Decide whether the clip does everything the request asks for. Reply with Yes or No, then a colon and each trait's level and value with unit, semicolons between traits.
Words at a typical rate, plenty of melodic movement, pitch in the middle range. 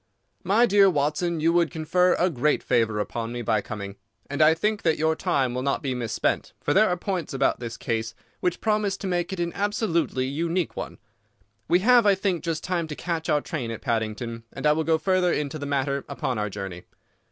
No: fast, 215 wpm; wide, 6.3 semitones; medium, 160 Hz